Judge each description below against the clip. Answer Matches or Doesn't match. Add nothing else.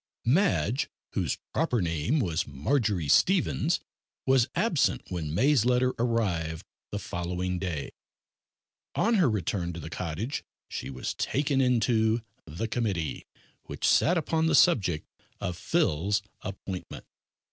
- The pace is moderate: Doesn't match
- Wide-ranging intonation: Matches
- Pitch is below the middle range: Matches